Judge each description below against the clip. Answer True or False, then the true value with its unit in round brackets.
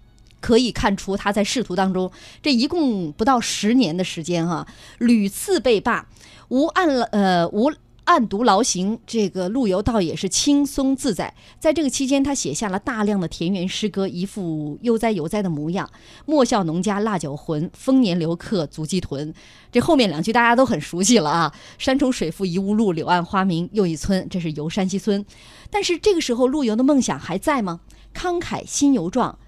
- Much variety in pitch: True (6.5 semitones)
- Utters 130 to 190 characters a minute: False (275 characters per minute)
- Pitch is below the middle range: False (205 Hz)